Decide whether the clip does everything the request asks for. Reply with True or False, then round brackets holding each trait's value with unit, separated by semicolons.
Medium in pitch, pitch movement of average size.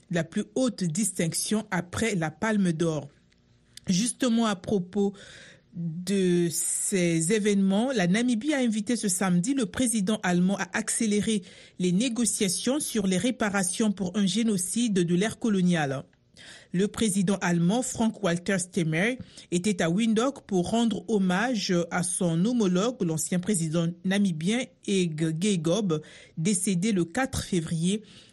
False (195 Hz; 3.9 semitones)